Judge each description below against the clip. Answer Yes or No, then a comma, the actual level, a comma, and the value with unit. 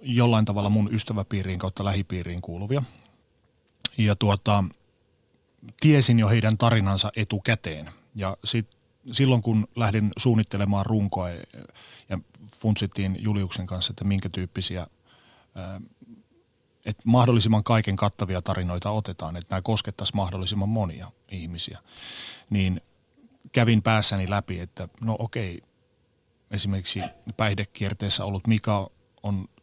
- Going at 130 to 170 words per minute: No, average, 105 wpm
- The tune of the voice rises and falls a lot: No, average, 2.8 semitones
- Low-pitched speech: Yes, low, 105 Hz